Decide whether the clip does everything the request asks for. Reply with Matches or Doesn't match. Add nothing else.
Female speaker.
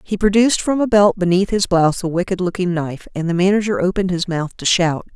Matches